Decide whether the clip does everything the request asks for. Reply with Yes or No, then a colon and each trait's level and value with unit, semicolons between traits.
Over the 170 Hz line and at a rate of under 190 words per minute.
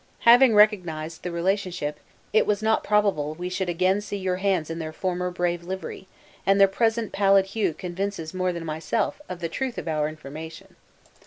Yes: medium, 185 Hz; average, 180 wpm